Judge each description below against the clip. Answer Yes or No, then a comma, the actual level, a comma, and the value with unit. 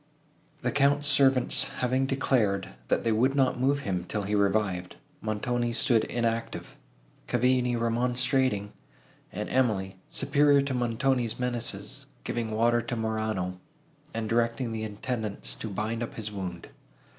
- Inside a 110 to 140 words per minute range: Yes, slow, 135 wpm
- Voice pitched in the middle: No, low, 115 Hz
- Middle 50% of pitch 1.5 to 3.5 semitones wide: Yes, average, 3.0 semitones